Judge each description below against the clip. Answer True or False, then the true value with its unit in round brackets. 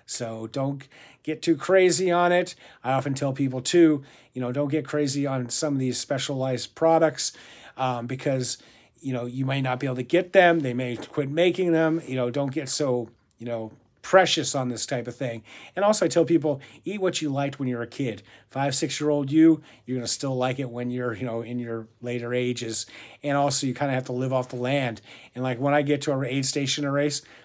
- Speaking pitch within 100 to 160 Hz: True (135 Hz)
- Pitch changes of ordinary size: True (3.3 semitones)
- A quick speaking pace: True (235 wpm)